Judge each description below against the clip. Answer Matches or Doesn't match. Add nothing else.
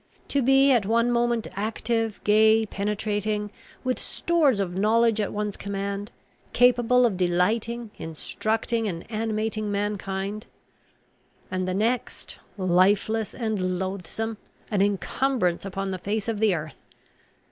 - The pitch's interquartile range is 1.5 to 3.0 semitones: Matches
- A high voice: Matches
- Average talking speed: Doesn't match